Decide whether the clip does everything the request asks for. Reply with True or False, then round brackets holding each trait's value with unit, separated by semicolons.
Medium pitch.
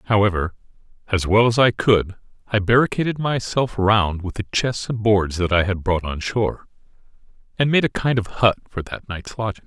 False (105 Hz)